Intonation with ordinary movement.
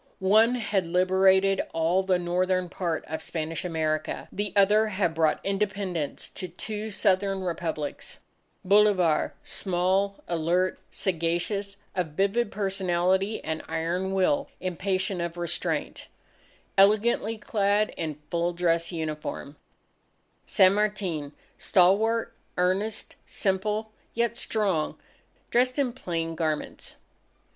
Yes: average, 3.2 semitones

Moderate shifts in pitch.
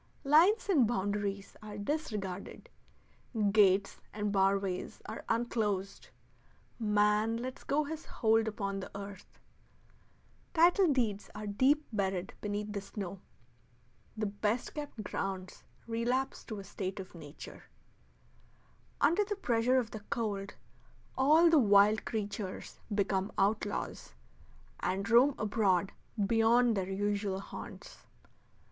Yes: average, 3.3 semitones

